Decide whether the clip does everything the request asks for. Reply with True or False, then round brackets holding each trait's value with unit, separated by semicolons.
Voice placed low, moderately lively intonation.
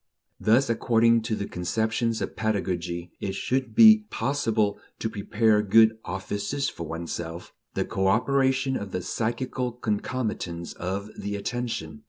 True (110 Hz; 4.1 semitones)